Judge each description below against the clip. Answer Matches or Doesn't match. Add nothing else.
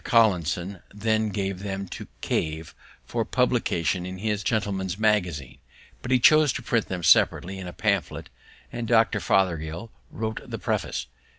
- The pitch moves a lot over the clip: Doesn't match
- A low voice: Matches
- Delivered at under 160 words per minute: Matches